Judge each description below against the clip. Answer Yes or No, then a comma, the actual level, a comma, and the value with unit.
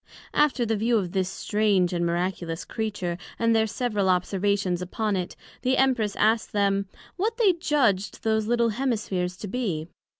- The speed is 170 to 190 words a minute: No, average, 160 wpm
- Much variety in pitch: No, average, 4.0 semitones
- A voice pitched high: Yes, high, 210 Hz